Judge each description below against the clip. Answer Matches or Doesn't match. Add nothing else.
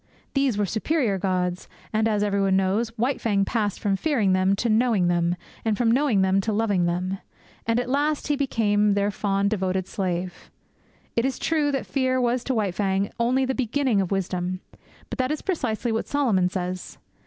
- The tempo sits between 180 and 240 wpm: Matches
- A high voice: Matches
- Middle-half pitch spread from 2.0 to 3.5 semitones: Doesn't match